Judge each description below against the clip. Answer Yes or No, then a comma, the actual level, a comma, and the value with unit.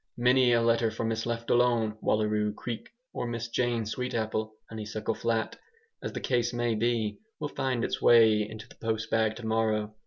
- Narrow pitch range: Yes, narrow, 1.6 semitones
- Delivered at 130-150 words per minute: No, average, 165 wpm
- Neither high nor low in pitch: No, low, 115 Hz